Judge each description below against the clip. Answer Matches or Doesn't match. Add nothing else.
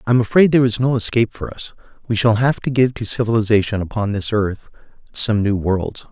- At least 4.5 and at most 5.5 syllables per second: Doesn't match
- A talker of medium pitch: Doesn't match